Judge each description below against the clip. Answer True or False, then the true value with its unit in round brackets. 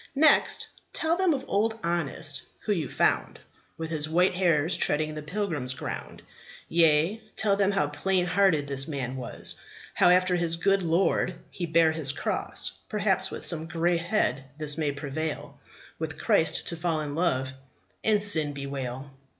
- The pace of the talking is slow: False (160 wpm)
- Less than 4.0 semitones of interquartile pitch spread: False (4.3 semitones)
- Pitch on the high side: False (165 Hz)